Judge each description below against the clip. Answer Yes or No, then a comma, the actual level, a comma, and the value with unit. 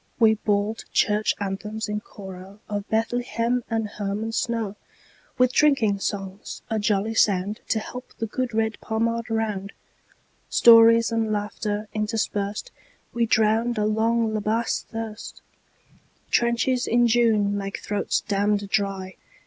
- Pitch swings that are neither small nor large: No, narrow, 2.0 semitones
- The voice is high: Yes, high, 220 Hz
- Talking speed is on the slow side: Yes, slow, 110 wpm